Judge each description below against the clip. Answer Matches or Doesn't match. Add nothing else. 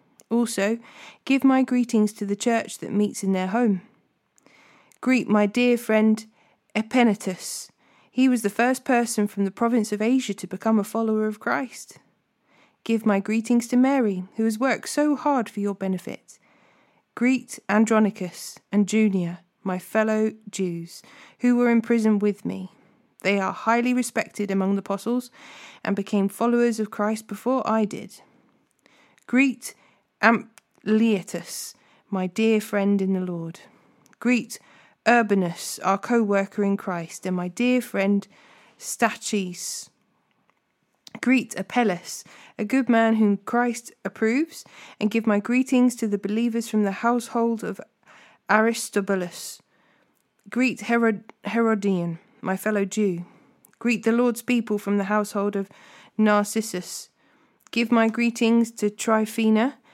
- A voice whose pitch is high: Matches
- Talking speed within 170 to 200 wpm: Doesn't match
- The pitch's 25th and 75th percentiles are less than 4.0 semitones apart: Matches